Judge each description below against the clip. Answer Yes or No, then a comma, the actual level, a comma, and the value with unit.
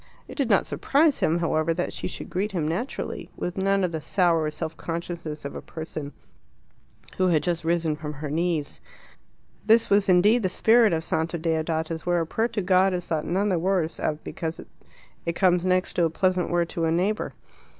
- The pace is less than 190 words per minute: No, average, 200 wpm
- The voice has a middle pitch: Yes, medium, 175 Hz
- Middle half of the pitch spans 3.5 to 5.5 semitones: No, average, 2.7 semitones